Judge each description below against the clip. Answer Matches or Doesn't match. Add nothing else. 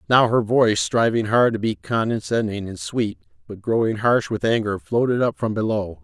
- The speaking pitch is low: Matches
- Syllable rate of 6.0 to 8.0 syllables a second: Doesn't match